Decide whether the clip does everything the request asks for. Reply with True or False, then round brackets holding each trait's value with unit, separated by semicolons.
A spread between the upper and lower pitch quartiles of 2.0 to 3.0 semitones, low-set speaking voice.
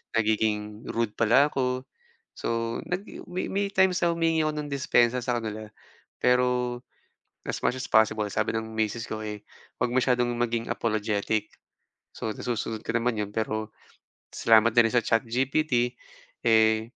True (2.5 semitones; 115 Hz)